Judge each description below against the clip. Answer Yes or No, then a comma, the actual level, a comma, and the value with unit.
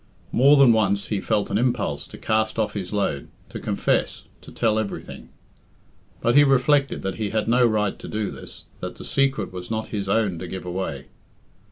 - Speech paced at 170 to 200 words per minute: Yes, average, 195 wpm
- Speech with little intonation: No, average, 3.5 semitones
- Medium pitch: No, low, 110 Hz